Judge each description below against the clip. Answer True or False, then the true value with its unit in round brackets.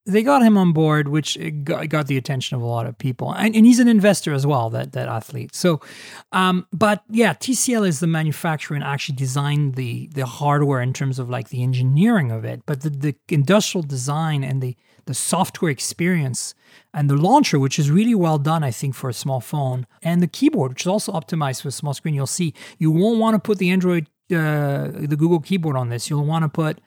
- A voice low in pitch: False (150 Hz)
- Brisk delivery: True (225 wpm)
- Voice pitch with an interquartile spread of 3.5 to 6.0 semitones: True (4.9 semitones)